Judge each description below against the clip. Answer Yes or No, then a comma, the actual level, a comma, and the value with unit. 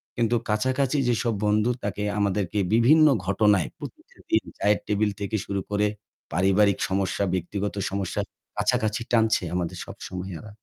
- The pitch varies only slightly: Yes, narrow, 2.2 semitones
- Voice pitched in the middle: No, low, 105 Hz